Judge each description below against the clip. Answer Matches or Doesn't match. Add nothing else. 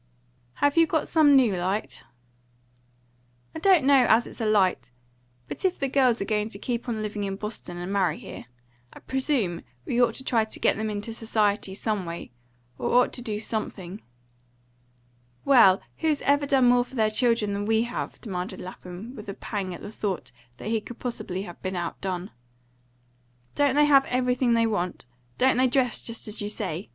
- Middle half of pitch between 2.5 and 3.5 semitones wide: Doesn't match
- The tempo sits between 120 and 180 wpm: Doesn't match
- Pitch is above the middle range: Matches